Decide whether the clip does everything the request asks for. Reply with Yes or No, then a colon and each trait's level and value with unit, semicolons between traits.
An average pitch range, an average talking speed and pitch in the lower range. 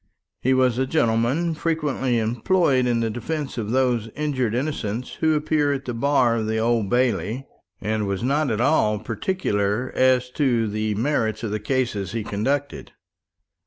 Yes: average, 4.1 semitones; average, 160 wpm; low, 125 Hz